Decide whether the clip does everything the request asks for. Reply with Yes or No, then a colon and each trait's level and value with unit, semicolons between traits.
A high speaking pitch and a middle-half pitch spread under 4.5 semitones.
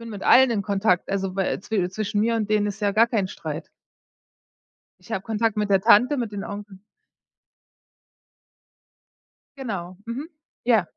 Yes: high, 210 Hz; average, 2.7 semitones